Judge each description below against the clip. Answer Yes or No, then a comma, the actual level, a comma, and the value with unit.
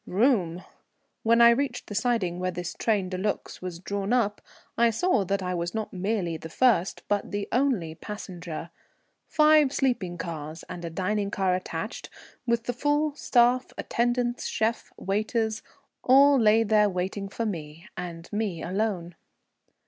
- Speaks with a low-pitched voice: No, high, 205 Hz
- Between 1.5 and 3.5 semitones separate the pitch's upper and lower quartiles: No, average, 4.7 semitones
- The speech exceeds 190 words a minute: No, average, 155 wpm